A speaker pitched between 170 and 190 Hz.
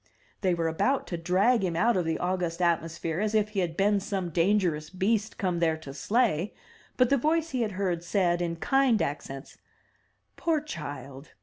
Yes: medium, 185 Hz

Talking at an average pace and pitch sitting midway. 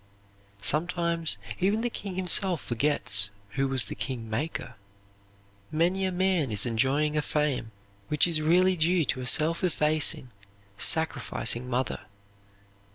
No: slow, 125 wpm; medium, 155 Hz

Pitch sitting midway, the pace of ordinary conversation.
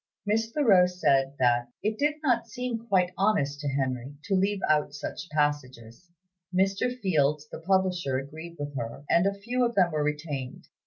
Yes: medium, 170 Hz; average, 170 wpm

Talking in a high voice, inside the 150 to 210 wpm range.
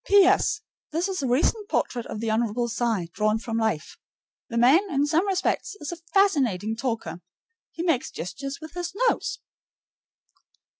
Yes: very high, 270 Hz; average, 155 wpm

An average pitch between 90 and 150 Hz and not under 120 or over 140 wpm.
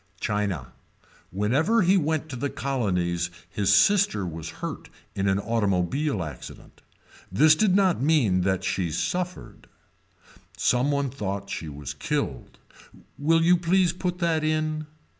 Yes: low, 135 Hz; slow, 135 wpm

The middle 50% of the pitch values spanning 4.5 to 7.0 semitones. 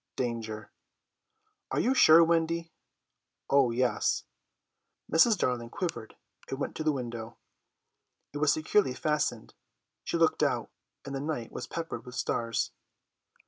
Yes: wide, 5.5 semitones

